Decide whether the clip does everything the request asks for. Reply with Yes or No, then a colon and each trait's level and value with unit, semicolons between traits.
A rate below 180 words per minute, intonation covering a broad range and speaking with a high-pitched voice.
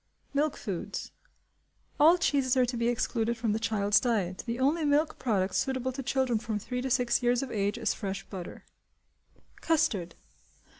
No: average, 165 wpm; average, 4.0 semitones; high, 240 Hz